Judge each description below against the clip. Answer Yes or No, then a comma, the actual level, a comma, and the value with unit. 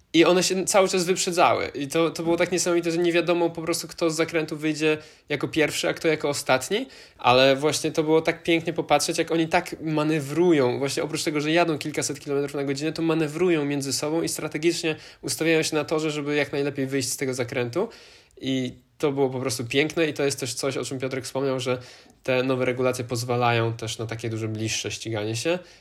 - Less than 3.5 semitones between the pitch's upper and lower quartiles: No, average, 3.8 semitones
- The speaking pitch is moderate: Yes, medium, 150 Hz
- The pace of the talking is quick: Yes, fast, 210 wpm